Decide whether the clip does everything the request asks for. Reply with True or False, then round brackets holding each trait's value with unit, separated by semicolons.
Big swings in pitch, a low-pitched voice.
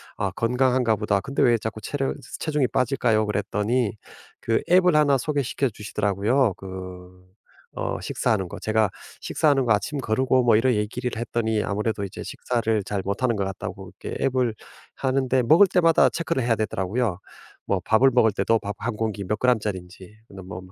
False (4.0 semitones; 110 Hz)